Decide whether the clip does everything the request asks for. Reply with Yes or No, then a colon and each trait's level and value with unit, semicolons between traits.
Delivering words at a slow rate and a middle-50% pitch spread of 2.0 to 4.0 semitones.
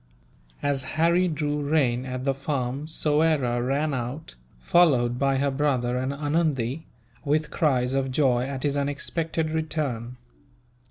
Yes: slow, 130 wpm; average, 3.2 semitones